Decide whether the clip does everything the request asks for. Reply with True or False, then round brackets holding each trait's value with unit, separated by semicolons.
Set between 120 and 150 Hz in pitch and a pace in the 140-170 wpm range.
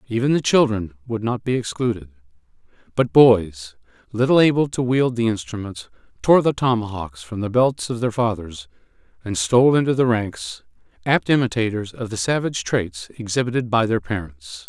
False (110 Hz; 160 wpm)